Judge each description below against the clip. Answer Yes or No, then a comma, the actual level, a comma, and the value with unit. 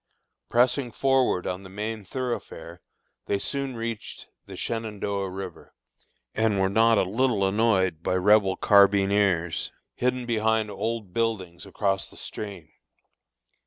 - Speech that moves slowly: Yes, slow, 125 wpm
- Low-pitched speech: Yes, low, 105 Hz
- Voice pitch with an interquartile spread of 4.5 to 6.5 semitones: No, average, 3.1 semitones